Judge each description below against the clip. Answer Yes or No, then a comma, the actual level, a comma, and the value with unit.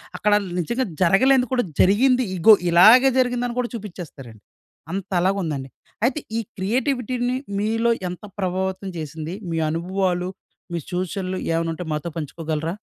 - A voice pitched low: No, high, 190 Hz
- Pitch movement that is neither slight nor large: No, wide, 6.0 semitones